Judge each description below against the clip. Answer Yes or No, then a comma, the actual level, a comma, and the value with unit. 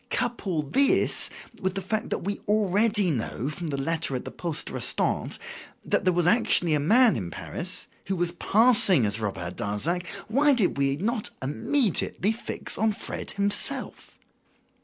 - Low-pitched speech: No, medium, 180 Hz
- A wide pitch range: Yes, wide, 6.7 semitones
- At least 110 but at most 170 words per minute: Yes, average, 155 wpm